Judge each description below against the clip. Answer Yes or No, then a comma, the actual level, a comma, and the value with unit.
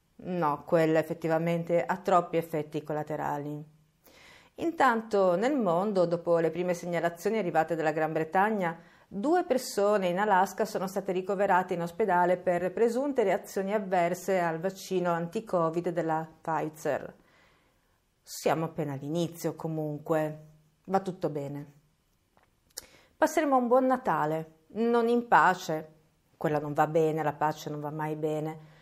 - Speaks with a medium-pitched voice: Yes, medium, 170 Hz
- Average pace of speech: Yes, average, 125 wpm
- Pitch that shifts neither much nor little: Yes, average, 3.6 semitones